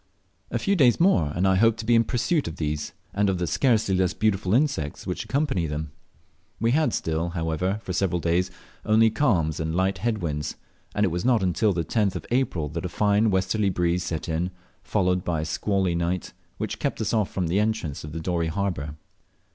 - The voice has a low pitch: Yes, very low, 95 Hz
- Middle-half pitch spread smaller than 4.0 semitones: No, average, 4.6 semitones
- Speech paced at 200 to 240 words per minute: Yes, fast, 205 wpm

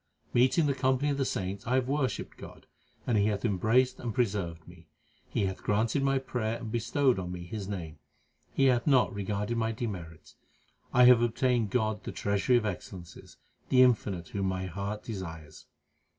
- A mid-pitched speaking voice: No, low, 110 Hz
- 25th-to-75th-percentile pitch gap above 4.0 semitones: Yes, average, 4.7 semitones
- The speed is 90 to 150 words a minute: No, average, 180 wpm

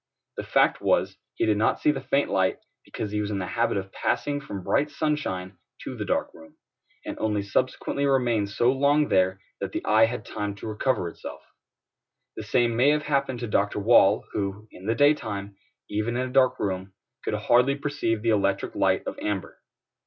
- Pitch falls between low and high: No, low, 110 Hz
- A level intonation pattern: No, average, 5.0 semitones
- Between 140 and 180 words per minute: No, average, 195 wpm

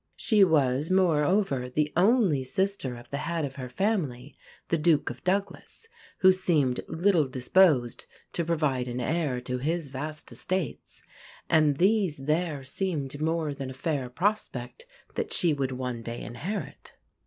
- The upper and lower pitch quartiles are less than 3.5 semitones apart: No, wide, 5.6 semitones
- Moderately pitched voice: Yes, medium, 150 Hz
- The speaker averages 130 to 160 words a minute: Yes, average, 150 wpm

